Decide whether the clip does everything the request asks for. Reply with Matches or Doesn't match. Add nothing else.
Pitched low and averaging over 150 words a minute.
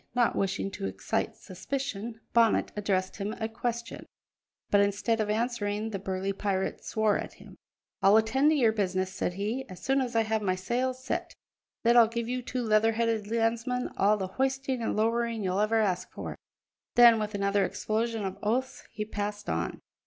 Doesn't match